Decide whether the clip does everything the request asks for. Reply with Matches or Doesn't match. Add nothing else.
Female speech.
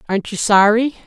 Matches